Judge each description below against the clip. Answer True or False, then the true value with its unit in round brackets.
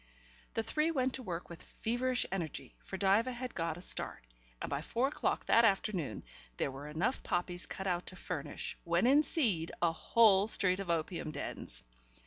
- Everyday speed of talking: True (180 wpm)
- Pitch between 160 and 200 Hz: True (190 Hz)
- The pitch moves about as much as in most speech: False (5.9 semitones)